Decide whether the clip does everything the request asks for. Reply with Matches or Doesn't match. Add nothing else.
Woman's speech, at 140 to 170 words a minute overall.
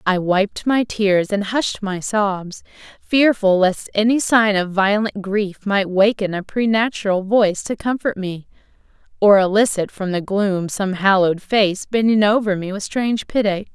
Matches